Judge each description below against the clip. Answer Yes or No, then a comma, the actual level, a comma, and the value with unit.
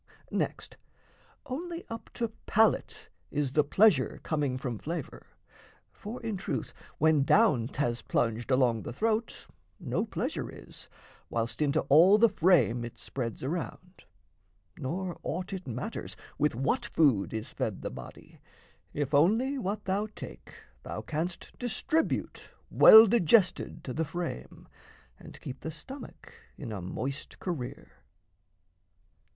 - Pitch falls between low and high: Yes, medium, 155 Hz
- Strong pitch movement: Yes, wide, 8.1 semitones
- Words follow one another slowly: Yes, slow, 130 wpm